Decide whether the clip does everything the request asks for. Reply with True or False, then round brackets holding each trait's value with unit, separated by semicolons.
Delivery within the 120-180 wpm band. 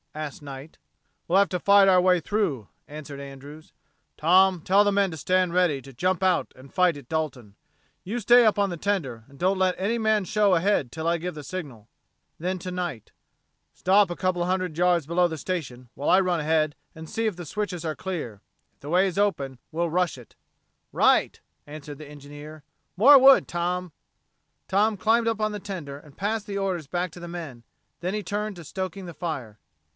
False (205 wpm)